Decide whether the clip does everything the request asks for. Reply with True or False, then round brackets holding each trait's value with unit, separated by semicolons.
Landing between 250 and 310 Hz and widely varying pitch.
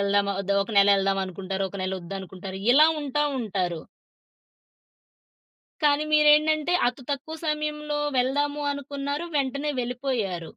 True (260 Hz; 7.2 semitones)